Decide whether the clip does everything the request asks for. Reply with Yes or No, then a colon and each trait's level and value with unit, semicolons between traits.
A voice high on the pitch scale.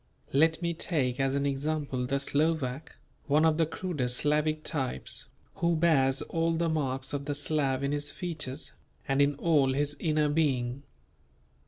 No: medium, 145 Hz